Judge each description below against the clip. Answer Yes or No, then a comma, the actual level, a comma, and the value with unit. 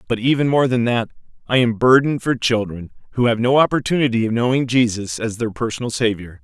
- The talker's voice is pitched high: No, low, 120 Hz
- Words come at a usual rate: Yes, average, 195 wpm